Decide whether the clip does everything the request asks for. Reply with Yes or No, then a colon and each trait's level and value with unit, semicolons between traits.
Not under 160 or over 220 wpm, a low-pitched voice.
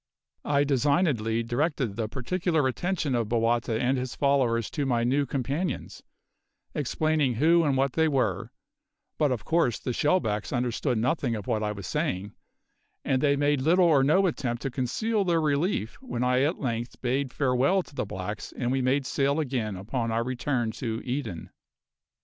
Yes: average, 170 wpm; low, 130 Hz